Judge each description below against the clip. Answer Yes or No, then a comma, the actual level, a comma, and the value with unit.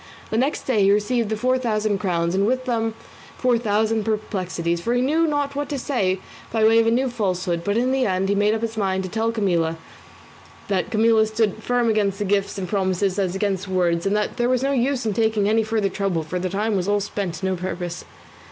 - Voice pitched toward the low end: No, high, 210 Hz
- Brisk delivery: Yes, fast, 235 wpm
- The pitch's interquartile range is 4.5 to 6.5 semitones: No, average, 3.4 semitones